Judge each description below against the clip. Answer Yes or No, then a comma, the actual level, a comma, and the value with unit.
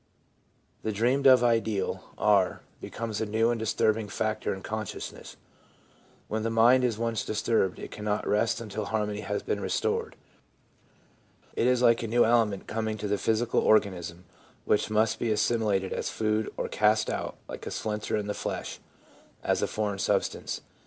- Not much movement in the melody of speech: Yes, narrow, 1.6 semitones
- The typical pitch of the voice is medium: No, low, 110 Hz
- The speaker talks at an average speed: Yes, average, 165 wpm